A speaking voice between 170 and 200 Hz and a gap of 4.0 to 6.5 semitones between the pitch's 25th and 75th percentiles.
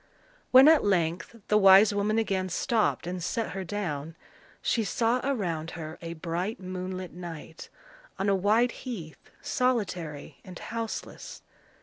Yes: high, 190 Hz; average, 4.6 semitones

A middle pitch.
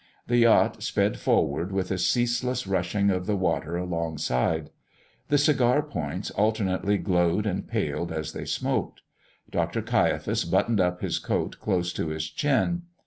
No: very low, 95 Hz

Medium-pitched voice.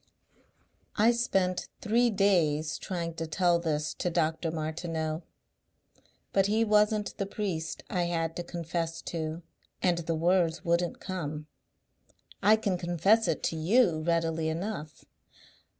Yes: medium, 170 Hz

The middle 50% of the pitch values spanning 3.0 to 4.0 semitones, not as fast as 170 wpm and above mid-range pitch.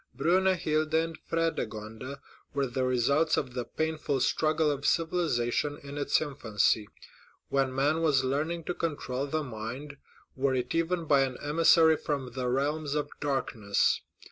No: average, 3.6 semitones; average, 140 wpm; medium, 145 Hz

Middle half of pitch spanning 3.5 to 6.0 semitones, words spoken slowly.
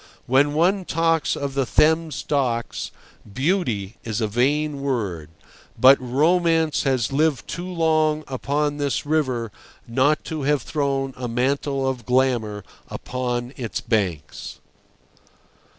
Yes: average, 4.0 semitones; slow, 120 wpm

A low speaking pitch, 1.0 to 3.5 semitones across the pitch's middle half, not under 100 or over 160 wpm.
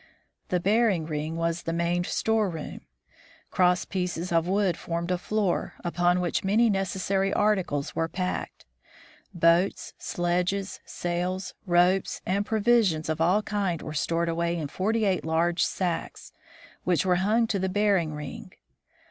No: medium, 180 Hz; narrow, 2.6 semitones; average, 145 wpm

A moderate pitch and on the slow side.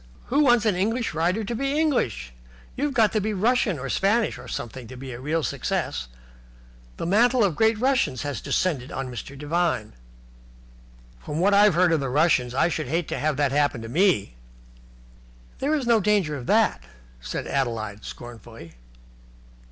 No: medium, 165 Hz; average, 175 wpm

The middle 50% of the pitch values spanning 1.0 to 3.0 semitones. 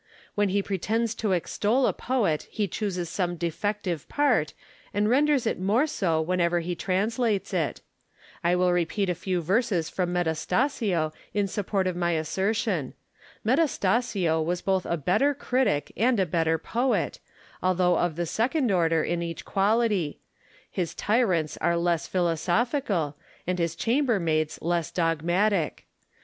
No: average, 4.5 semitones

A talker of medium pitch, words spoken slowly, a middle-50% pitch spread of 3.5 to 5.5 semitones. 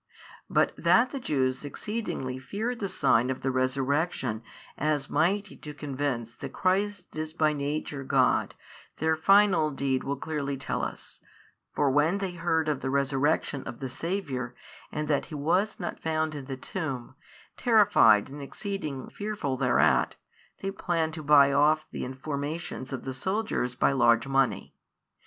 No: medium, 145 Hz; average, 155 wpm; average, 4.2 semitones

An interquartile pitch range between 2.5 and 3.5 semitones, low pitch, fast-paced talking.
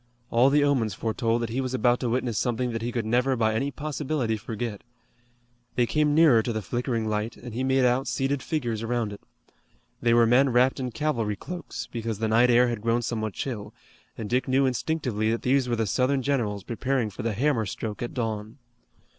Yes: average, 2.8 semitones; low, 120 Hz; fast, 210 wpm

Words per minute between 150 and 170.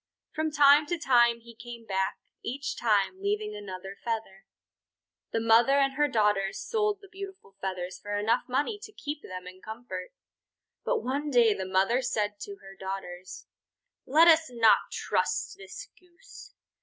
Yes: average, 155 wpm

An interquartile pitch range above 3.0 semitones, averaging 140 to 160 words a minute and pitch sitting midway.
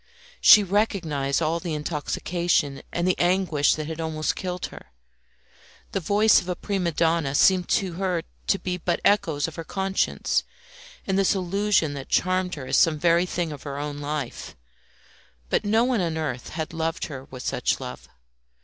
No: average, 3.6 semitones; average, 175 wpm; medium, 170 Hz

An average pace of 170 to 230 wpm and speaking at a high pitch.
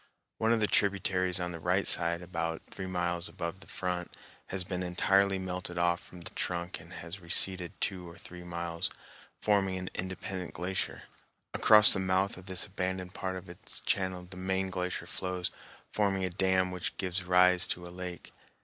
No: average, 180 wpm; very low, 90 Hz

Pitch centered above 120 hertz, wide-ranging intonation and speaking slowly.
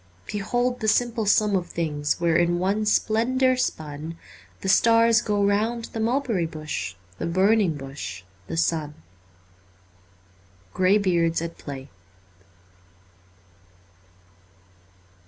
Yes: medium, 185 Hz; wide, 6.4 semitones; slow, 110 wpm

